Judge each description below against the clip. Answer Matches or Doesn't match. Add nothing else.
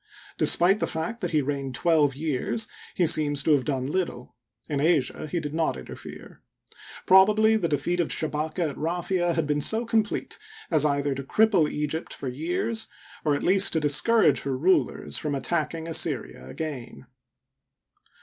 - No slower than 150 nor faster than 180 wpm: Matches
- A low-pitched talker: Doesn't match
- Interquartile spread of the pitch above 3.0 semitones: Matches